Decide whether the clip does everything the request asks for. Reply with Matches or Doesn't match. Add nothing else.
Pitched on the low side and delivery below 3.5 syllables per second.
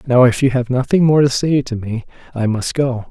Doesn't match